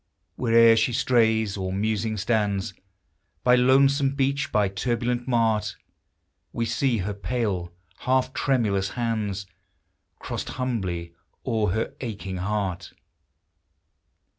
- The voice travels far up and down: No, average, 3.7 semitones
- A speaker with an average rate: No, slow, 105 wpm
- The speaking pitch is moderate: No, low, 110 Hz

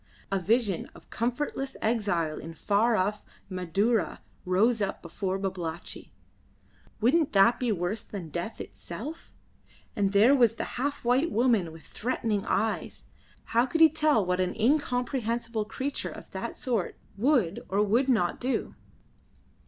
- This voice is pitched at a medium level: No, high, 220 Hz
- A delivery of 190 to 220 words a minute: No, average, 140 wpm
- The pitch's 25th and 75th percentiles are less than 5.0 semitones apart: Yes, average, 4.6 semitones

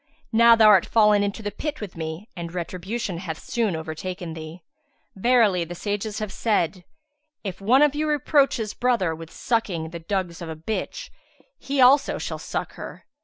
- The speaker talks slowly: No, average, 175 wpm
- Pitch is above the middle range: Yes, high, 200 Hz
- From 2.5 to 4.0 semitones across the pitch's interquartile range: No, average, 5.2 semitones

